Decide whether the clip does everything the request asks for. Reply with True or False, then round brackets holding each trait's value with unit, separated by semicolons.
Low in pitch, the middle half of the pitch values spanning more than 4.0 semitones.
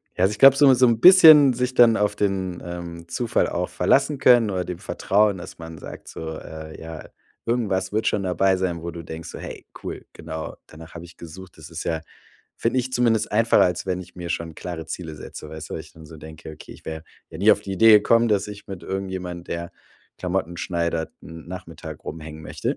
True (90 Hz; 4.6 semitones)